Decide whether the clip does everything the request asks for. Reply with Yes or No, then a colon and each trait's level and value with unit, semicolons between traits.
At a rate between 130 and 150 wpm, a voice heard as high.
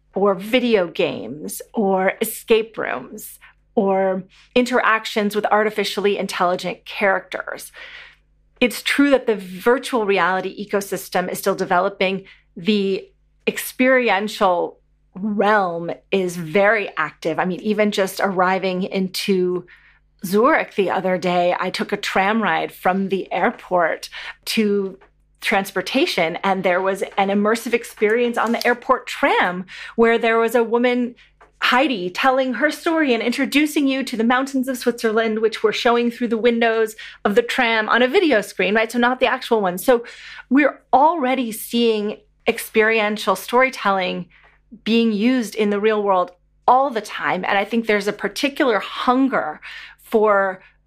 Yes: average, 140 wpm; high, 215 Hz